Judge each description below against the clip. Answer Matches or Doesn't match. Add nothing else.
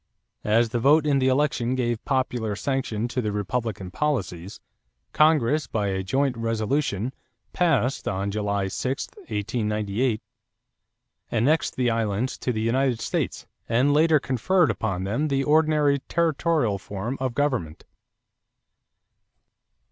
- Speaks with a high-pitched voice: Doesn't match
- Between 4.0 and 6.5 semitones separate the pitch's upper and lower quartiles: Matches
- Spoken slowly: Matches